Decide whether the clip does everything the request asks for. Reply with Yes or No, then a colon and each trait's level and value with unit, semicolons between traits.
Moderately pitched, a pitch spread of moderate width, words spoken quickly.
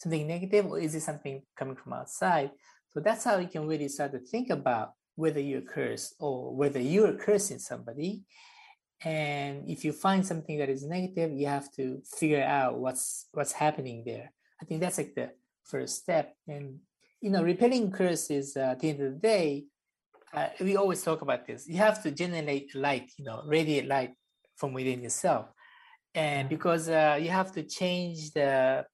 No: medium, 155 Hz; average, 4.2 semitones; average, 185 wpm